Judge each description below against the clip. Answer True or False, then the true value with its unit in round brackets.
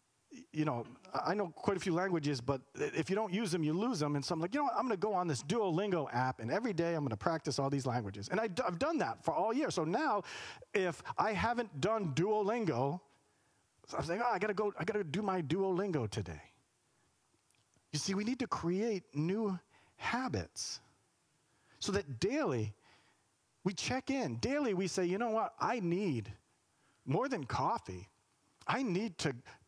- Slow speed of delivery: False (200 wpm)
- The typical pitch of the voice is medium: True (175 Hz)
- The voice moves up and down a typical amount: False (7.3 semitones)